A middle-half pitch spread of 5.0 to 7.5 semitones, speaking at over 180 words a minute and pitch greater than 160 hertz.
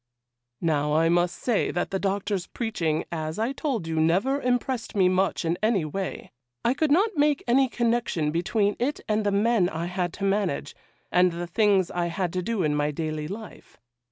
Yes: wide, 5.5 semitones; average, 190 wpm; high, 190 Hz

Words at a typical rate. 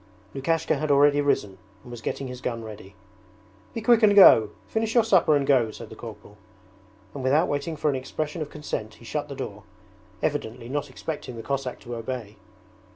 Yes: average, 190 wpm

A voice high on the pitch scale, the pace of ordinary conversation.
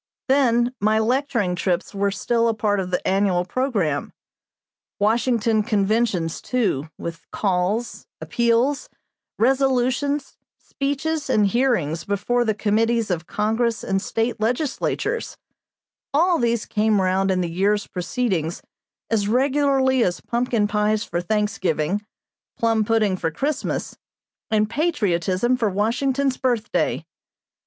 No: high, 220 Hz; slow, 115 wpm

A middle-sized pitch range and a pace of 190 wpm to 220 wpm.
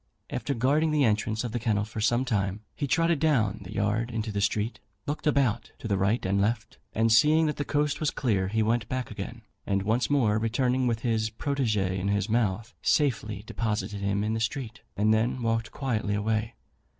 Yes: average, 3.4 semitones; average, 200 wpm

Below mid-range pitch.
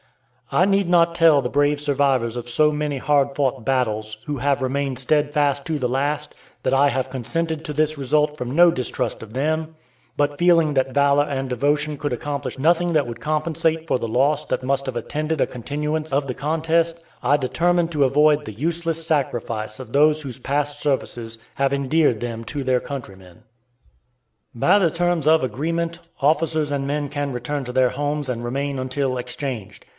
No: medium, 145 Hz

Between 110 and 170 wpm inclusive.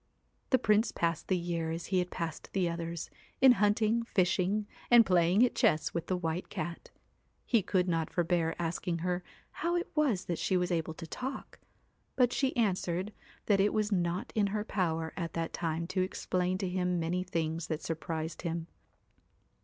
No: average, 185 wpm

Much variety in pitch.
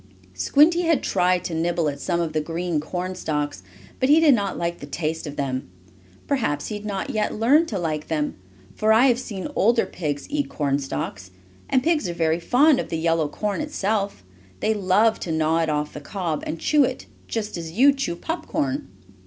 Yes: wide, 6.6 semitones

